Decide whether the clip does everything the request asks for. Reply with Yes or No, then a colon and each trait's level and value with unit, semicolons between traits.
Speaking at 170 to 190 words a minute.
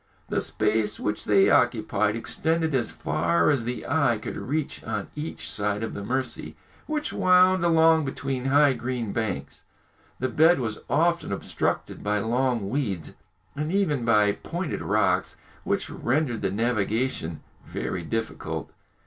No: average, 140 wpm